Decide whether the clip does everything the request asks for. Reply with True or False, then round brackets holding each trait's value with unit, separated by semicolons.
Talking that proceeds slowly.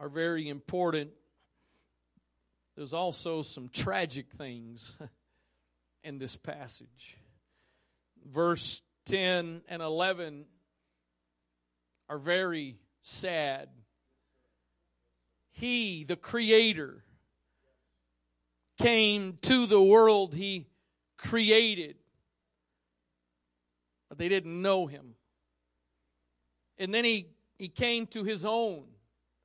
True (80 wpm)